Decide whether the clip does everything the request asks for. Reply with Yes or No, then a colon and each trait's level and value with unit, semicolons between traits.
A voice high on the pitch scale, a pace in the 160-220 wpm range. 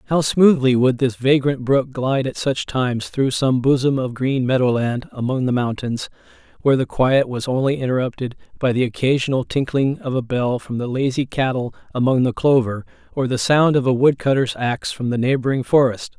No: low, 130 Hz; average, 185 wpm